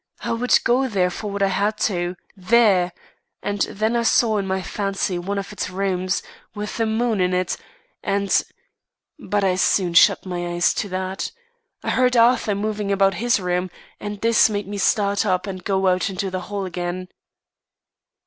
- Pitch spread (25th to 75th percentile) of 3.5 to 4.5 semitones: No, narrow, 2.4 semitones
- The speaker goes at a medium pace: Yes, average, 185 wpm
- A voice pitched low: No, high, 195 Hz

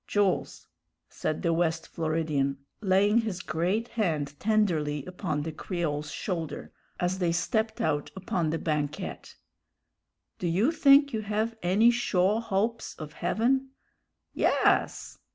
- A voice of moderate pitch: Yes, medium, 180 Hz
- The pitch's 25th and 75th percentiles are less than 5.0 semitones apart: No, wide, 5.4 semitones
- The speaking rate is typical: No, slow, 125 wpm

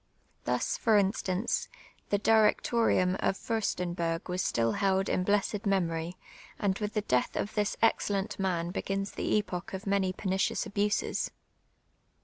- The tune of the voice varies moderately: No, narrow, 2.3 semitones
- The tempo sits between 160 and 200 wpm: No, average, 140 wpm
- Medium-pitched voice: No, high, 195 Hz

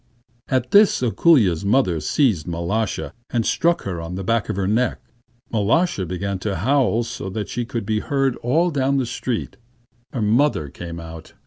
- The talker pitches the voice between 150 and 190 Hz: No, low, 110 Hz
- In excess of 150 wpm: Yes, average, 175 wpm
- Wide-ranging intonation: Yes, wide, 6.1 semitones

